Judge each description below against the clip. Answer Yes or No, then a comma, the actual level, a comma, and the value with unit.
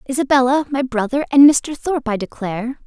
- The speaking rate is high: No, average, 170 wpm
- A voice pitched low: No, very high, 260 Hz